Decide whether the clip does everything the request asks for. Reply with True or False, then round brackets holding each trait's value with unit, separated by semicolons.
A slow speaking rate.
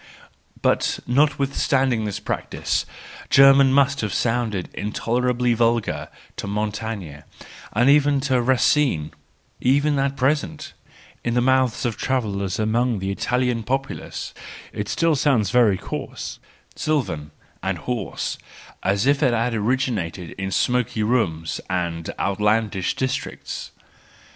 True (120 wpm)